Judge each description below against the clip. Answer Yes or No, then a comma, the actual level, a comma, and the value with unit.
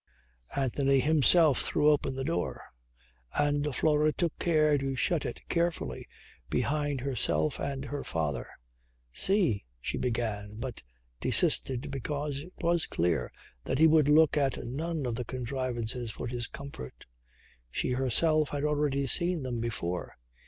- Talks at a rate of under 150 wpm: Yes, average, 140 wpm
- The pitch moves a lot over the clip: No, average, 3.9 semitones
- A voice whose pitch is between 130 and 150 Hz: Yes, medium, 140 Hz